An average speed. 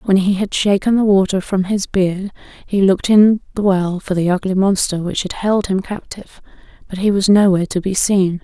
No: fast, 215 wpm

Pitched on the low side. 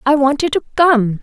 No: very high, 270 Hz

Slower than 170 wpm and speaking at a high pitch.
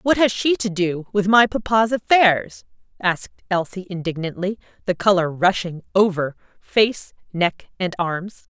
Yes: average, 140 wpm; high, 195 Hz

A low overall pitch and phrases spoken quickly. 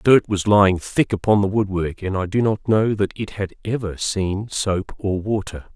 Yes: low, 100 Hz; fast, 220 wpm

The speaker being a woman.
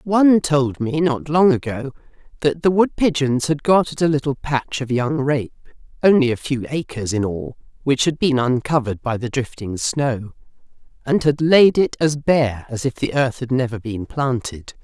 Yes: female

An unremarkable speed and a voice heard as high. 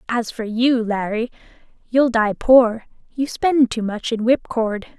Yes: average, 155 wpm; high, 235 Hz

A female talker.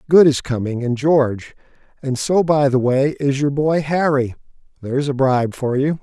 No: male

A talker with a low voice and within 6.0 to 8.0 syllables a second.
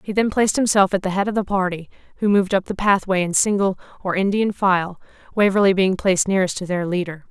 No: high, 190 Hz; 6.4 syllables/s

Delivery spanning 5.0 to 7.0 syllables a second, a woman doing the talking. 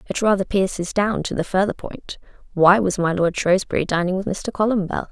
Yes: 5.5 syllables/s; female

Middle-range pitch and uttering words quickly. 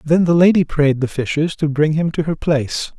Yes: medium, 155 Hz; fast, 240 wpm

